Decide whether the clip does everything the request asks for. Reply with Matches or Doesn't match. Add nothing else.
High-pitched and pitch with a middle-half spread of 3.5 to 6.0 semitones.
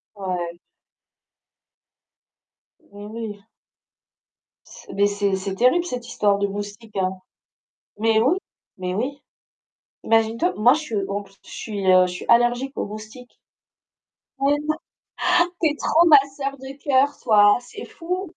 Matches